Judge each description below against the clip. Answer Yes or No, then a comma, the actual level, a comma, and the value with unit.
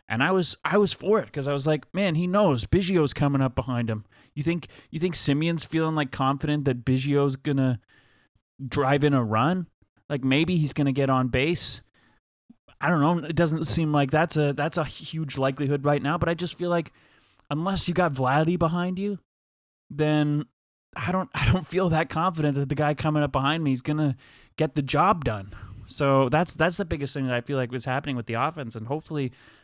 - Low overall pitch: No, medium, 145 Hz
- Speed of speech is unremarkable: No, fast, 215 wpm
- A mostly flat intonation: No, average, 3.7 semitones